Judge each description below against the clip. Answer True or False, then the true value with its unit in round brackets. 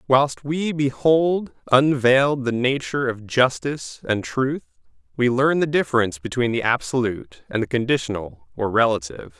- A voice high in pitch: False (125 Hz)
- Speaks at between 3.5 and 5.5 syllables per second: True (5.0 syllables/s)